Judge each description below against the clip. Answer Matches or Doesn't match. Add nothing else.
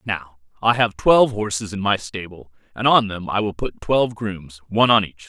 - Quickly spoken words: Matches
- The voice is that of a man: Matches